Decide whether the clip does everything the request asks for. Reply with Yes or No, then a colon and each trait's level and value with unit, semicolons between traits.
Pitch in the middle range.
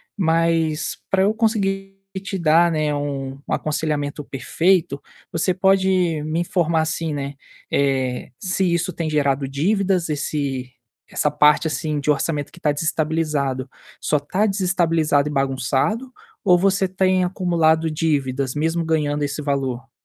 Yes: medium, 160 Hz